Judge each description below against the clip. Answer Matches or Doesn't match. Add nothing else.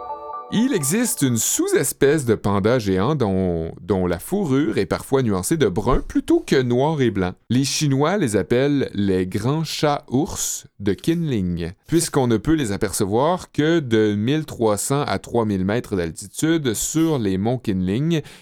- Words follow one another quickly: Doesn't match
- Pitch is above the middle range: Doesn't match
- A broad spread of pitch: Matches